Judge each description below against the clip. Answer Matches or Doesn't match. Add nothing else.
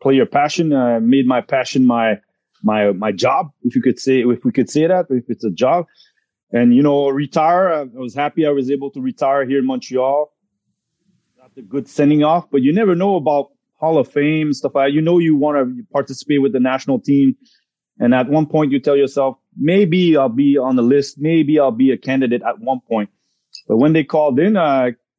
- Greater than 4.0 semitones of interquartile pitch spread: Doesn't match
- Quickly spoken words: Matches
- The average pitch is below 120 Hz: Doesn't match